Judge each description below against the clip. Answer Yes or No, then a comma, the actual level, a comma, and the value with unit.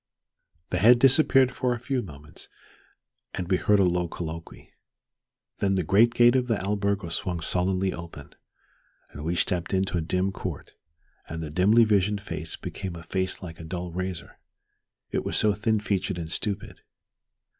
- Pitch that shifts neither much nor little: Yes, average, 3.4 semitones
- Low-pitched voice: Yes, very low, 95 Hz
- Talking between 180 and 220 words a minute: No, average, 165 wpm